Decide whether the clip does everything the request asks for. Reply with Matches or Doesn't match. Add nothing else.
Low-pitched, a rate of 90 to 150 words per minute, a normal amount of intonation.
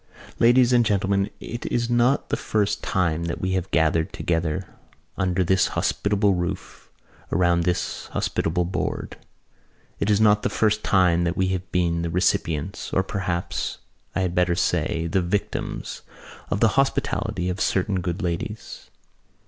Matches